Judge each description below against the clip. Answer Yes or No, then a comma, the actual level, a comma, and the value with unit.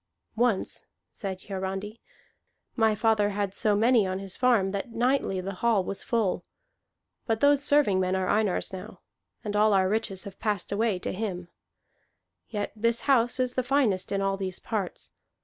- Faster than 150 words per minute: Yes, average, 165 wpm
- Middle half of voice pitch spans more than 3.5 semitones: No, average, 3.2 semitones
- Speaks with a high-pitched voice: Yes, high, 205 Hz